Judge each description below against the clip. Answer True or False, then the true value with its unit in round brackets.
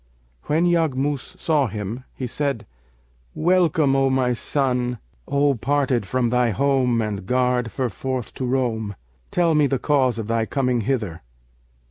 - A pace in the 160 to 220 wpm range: False (140 wpm)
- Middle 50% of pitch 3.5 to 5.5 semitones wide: False (3.1 semitones)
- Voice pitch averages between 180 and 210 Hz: False (130 Hz)